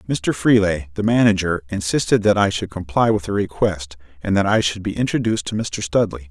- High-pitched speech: No, very low, 95 Hz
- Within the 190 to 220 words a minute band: Yes, average, 200 wpm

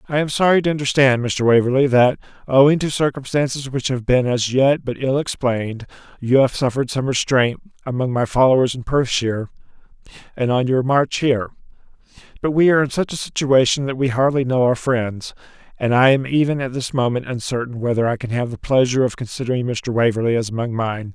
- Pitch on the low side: Yes, low, 130 Hz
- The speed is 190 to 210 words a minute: Yes, average, 195 wpm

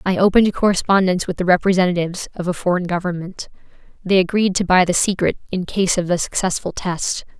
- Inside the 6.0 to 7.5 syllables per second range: Yes, 6.2 syllables/s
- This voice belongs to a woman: Yes, female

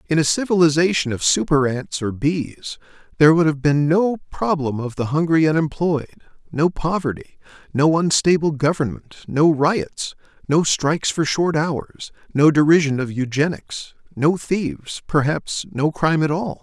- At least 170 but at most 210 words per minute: No, average, 150 wpm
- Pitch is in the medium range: Yes, medium, 150 Hz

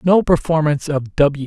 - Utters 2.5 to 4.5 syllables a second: No, 4.9 syllables/s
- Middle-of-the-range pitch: Yes, medium, 155 Hz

